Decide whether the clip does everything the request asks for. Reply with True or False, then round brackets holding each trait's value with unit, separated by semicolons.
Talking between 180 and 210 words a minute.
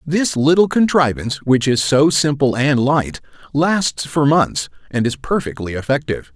False (150 wpm)